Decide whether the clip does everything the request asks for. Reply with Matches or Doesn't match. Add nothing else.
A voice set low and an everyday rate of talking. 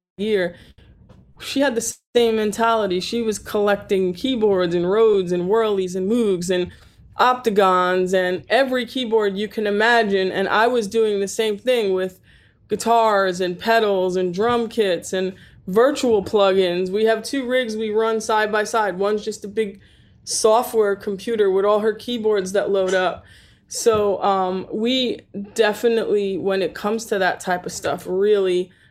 Doesn't match